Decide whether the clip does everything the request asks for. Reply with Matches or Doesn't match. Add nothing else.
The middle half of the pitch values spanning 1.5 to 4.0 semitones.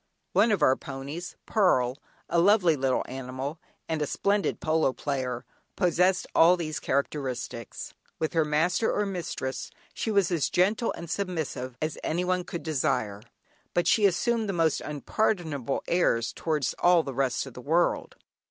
Doesn't match